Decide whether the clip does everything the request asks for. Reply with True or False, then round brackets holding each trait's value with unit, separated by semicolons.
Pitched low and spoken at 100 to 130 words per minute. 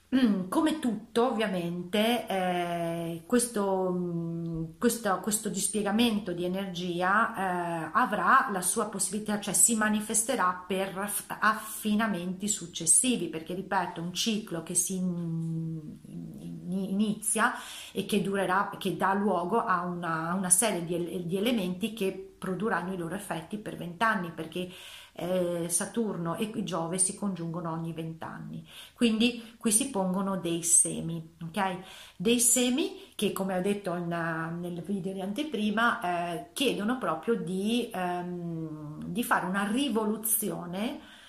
False (190 Hz; 125 wpm)